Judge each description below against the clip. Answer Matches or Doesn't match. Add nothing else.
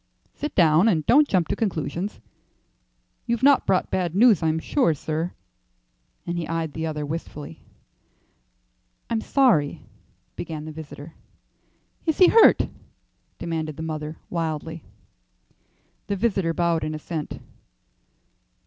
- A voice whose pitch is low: Doesn't match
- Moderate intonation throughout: Matches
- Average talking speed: Doesn't match